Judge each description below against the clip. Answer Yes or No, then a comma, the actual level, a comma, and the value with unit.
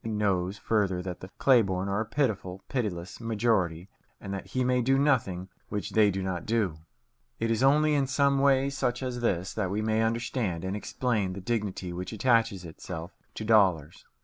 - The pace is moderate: Yes, average, 190 wpm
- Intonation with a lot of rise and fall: No, average, 4.7 semitones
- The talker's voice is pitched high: No, low, 105 Hz